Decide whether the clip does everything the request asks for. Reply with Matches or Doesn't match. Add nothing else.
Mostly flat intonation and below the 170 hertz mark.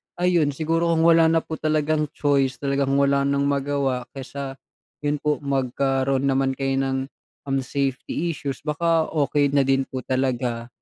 Matches